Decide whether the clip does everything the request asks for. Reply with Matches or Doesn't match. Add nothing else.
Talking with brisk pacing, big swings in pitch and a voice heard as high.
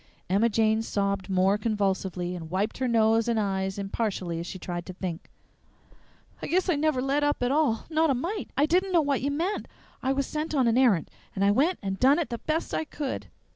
Matches